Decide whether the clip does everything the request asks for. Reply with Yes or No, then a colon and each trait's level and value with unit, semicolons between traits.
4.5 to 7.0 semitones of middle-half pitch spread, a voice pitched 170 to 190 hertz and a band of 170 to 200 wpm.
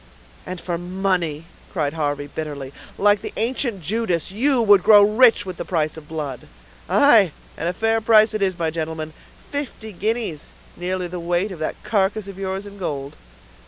Yes: average, 5.0 semitones; medium, 185 Hz; average, 175 wpm